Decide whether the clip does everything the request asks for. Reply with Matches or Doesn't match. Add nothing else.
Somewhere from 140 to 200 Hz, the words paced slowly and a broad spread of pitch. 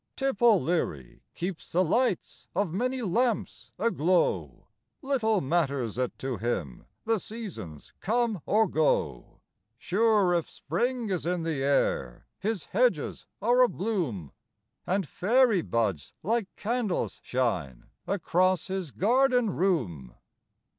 Matches